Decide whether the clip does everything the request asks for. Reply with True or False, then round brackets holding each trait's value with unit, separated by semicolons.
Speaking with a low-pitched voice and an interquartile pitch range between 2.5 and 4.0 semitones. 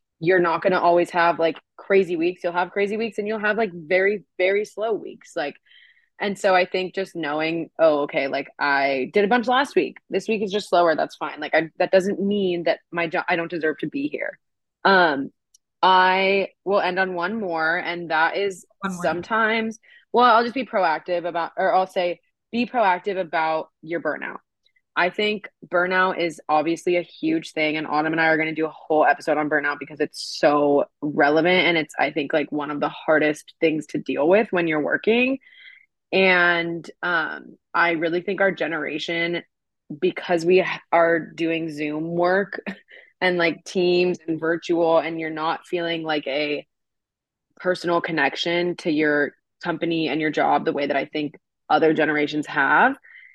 False (170 Hz; 3.3 semitones)